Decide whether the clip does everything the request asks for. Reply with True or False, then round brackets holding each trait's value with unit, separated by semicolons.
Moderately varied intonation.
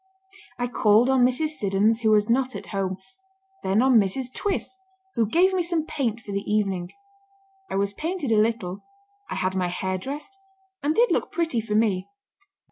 False (5.8 semitones)